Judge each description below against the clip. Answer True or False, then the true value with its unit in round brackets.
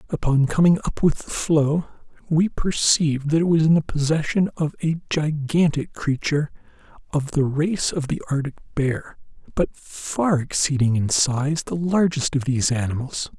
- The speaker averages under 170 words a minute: True (155 wpm)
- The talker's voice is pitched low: False (150 Hz)